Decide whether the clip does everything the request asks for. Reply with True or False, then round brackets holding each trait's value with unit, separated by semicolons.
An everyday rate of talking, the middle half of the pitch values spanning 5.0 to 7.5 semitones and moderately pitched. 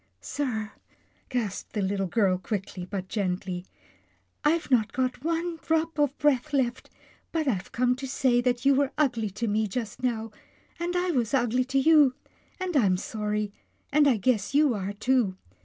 False (175 wpm; 5.3 semitones; 245 Hz)